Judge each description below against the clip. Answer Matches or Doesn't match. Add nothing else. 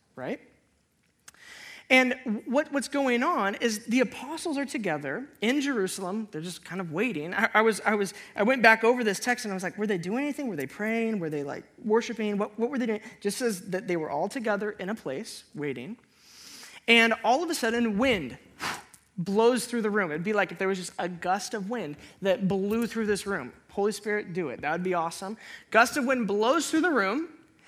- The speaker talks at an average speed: Doesn't match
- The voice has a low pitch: Doesn't match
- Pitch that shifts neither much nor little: Matches